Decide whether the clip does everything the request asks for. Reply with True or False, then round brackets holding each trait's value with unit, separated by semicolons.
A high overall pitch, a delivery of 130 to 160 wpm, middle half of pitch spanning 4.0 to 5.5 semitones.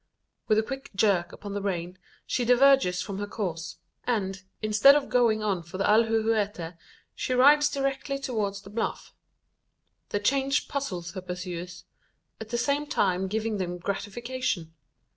True (210 Hz; 150 wpm; 5.1 semitones)